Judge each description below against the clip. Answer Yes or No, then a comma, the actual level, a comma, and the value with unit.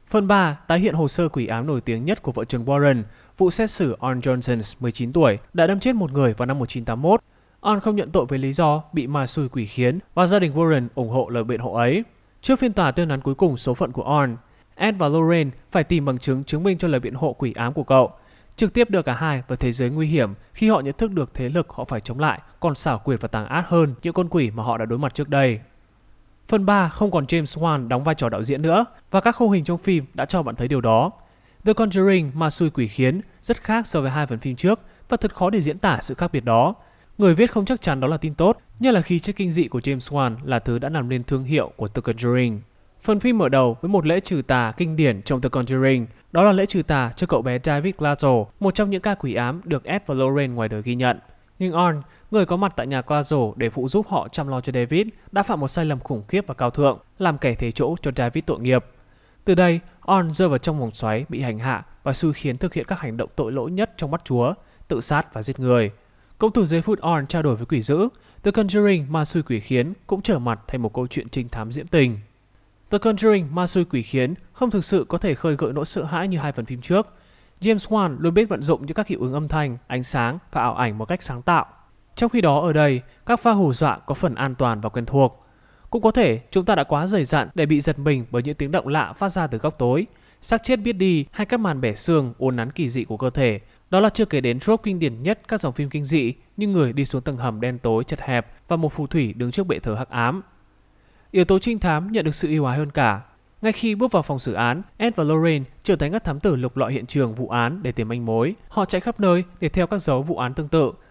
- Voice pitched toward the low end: No, medium, 150 Hz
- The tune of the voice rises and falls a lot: Yes, wide, 6.6 semitones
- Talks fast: Yes, fast, 270 wpm